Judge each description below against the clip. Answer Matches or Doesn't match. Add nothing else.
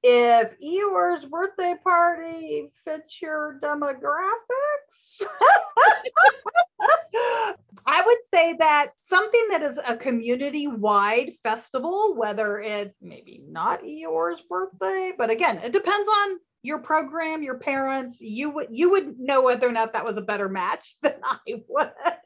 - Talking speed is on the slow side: Matches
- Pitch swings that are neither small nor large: Doesn't match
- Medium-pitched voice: Doesn't match